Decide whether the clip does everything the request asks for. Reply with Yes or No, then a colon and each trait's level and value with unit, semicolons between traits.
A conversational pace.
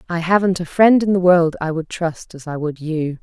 No: fast, 260 wpm